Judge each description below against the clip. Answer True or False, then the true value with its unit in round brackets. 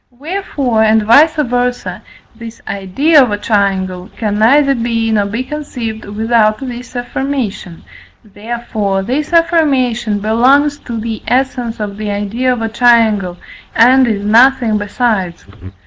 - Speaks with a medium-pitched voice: False (230 Hz)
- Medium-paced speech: False (130 wpm)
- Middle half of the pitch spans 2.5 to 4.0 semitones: True (3.5 semitones)